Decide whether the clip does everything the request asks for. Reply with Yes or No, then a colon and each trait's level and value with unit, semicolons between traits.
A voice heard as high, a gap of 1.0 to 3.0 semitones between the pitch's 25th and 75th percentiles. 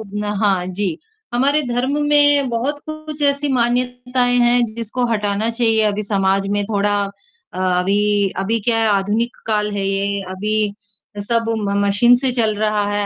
No: high, 215 Hz; average, 3.4 semitones